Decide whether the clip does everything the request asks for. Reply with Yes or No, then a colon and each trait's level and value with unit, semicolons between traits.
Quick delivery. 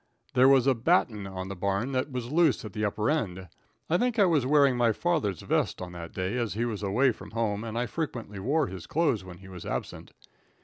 Yes: fast, 230 wpm